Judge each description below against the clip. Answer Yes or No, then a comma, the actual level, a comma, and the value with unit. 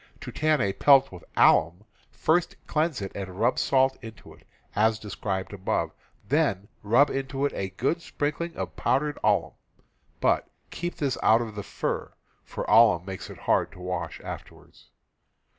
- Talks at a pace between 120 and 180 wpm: Yes, average, 160 wpm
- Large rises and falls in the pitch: Yes, wide, 6.6 semitones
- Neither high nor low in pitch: No, low, 115 Hz